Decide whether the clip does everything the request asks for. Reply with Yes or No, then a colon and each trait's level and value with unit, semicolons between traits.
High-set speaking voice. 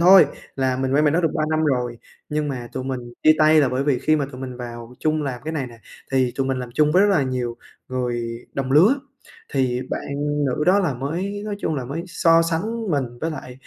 No: medium, 140 Hz